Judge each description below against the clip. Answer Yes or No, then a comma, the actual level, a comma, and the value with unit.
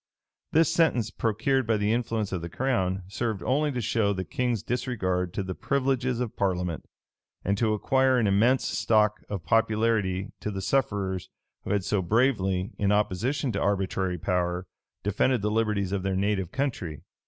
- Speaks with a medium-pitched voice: No, low, 105 Hz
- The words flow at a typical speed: Yes, average, 170 wpm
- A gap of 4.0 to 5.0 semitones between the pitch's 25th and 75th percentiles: Yes, average, 4.3 semitones